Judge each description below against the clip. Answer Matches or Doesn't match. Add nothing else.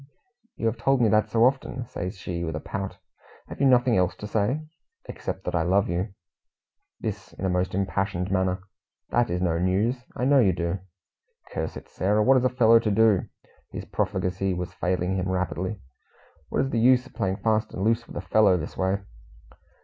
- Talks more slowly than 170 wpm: Doesn't match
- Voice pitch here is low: Matches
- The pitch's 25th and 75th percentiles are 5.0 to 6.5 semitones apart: Doesn't match